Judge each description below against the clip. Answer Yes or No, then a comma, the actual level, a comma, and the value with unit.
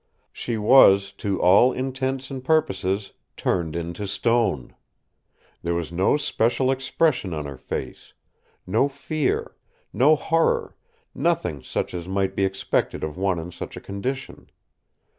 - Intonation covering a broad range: Yes, wide, 6.7 semitones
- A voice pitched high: No, low, 100 Hz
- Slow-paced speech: Yes, slow, 130 wpm